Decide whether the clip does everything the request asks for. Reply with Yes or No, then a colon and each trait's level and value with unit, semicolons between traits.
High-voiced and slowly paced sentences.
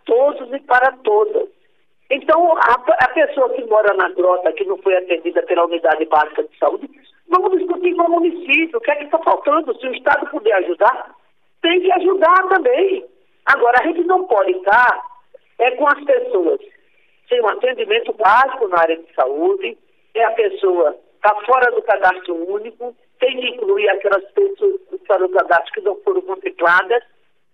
No: very high, 330 Hz; average, 175 wpm